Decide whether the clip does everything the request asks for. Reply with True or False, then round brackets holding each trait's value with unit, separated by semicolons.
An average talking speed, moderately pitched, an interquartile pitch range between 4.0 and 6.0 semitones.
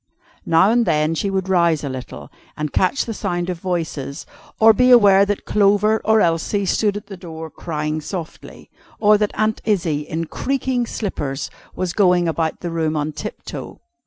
True (175 wpm; 180 Hz; 4.6 semitones)